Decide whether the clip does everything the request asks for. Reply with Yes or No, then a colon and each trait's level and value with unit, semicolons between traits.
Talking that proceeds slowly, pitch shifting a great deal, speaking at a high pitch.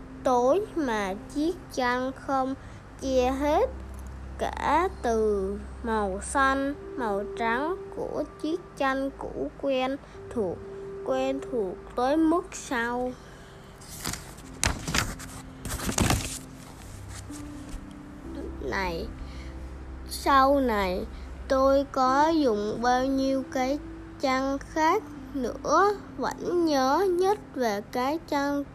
Yes: slow, 90 wpm; wide, 5.8 semitones; very high, 265 Hz